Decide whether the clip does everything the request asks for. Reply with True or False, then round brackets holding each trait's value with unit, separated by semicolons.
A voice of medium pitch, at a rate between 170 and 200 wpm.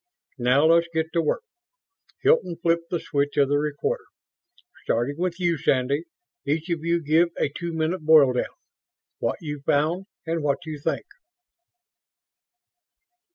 False (160 Hz; 145 wpm)